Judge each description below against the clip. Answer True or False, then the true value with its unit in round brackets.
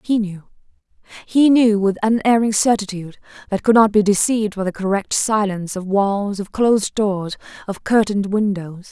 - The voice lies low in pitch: False (205 Hz)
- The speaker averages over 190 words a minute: False (170 wpm)